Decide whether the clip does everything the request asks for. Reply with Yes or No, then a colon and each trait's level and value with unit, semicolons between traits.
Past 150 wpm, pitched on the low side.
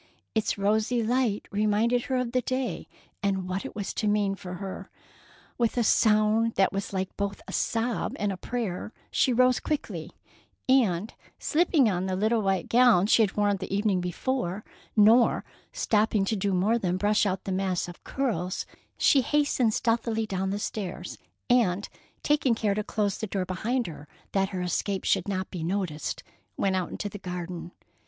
No: average, 175 wpm; high, 205 Hz